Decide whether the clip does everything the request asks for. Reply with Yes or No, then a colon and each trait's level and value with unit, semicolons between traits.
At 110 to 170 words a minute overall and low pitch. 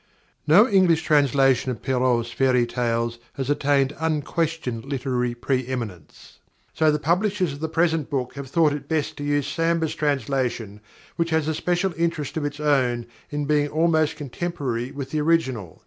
No: average, 165 wpm; medium, 145 Hz